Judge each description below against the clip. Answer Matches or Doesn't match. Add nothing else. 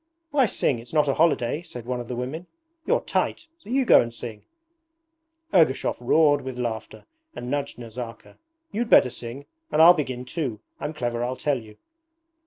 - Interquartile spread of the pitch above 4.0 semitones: Matches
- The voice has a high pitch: Doesn't match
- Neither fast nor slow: Matches